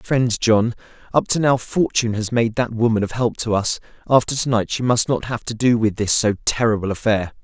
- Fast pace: Yes, fast, 225 wpm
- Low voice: Yes, low, 115 Hz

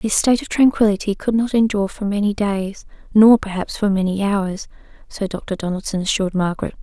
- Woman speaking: Yes, female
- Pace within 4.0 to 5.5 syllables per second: No, 5.8 syllables/s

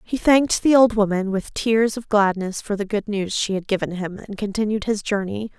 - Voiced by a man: No, female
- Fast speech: Yes, fast, 225 wpm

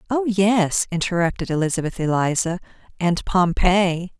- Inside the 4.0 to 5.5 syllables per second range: Yes, 4.6 syllables/s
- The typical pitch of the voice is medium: Yes, medium, 180 Hz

